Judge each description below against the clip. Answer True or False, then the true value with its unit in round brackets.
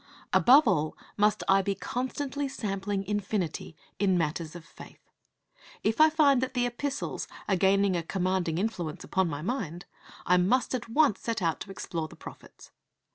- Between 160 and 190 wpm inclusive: True (165 wpm)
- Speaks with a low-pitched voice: False (195 Hz)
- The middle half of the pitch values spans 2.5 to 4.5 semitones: False (5.6 semitones)